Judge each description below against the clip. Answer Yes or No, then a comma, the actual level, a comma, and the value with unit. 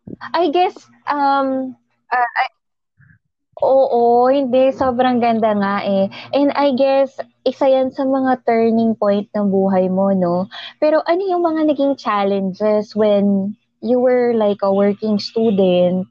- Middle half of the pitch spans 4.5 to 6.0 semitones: Yes, average, 5.1 semitones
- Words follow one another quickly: No, average, 140 wpm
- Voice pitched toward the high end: Yes, high, 230 Hz